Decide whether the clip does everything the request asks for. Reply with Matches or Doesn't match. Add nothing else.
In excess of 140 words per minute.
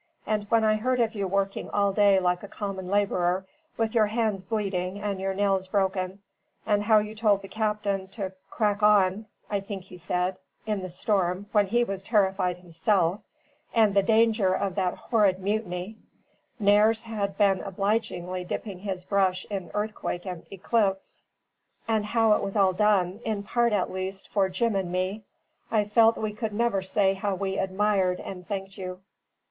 Matches